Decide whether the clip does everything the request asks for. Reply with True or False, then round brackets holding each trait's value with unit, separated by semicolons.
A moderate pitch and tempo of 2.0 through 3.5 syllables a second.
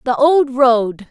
False (255 Hz; 3.1 syllables/s)